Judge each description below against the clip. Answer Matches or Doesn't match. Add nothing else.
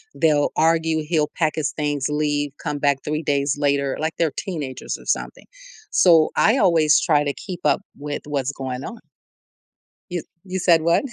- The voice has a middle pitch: Matches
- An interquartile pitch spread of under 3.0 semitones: Matches